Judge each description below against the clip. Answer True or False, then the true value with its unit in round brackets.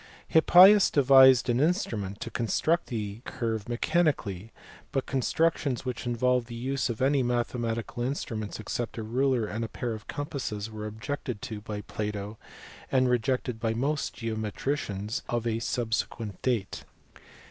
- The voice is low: True (120 Hz)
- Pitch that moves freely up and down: False (3.4 semitones)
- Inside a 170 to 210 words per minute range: False (145 wpm)